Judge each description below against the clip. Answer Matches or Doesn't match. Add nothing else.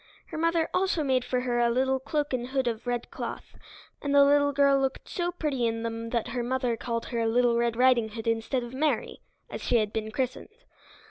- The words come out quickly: Matches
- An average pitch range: Matches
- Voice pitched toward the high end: Matches